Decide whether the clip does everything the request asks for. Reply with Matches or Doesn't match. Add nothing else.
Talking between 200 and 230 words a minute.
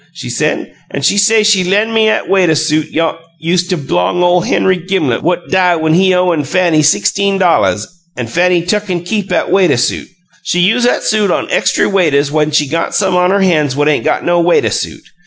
Matches